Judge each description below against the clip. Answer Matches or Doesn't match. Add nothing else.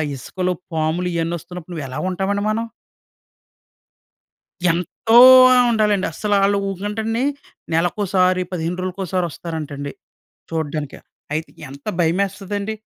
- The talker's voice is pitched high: Doesn't match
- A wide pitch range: Doesn't match